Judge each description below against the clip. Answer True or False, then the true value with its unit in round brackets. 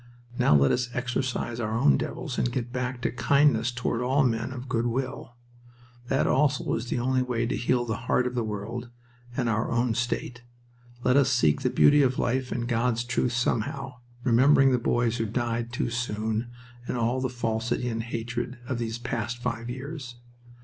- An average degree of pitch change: False (1.6 semitones)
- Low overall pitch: True (120 Hz)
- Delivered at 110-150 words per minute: False (185 wpm)